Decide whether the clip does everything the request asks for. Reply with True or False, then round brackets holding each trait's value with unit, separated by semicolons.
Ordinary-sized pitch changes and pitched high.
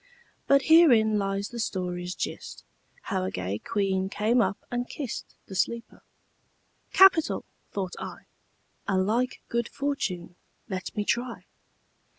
True (4.6 semitones; 210 Hz)